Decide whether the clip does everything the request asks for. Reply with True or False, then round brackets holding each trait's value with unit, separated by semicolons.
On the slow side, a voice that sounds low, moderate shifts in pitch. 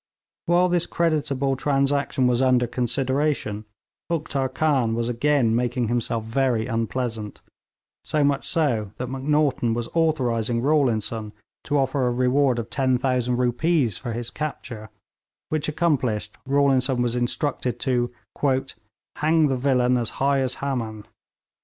True (130 wpm; 130 Hz; 3.1 semitones)